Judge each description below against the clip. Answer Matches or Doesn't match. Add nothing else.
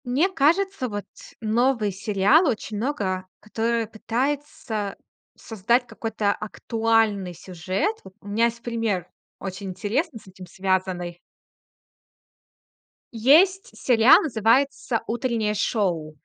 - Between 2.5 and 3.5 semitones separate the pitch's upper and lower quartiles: Doesn't match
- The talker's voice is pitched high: Matches